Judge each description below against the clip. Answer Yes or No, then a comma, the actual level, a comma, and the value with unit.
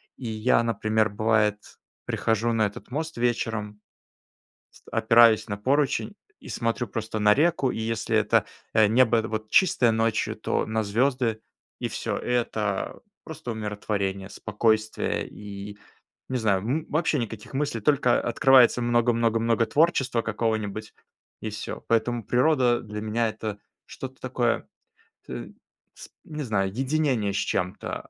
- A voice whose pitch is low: Yes, low, 115 Hz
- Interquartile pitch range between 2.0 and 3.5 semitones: Yes, narrow, 2.6 semitones